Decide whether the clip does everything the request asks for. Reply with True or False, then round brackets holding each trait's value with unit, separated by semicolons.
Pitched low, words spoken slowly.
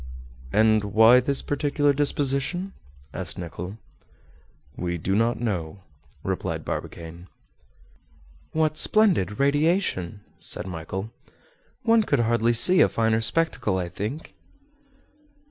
True (115 Hz; 105 wpm)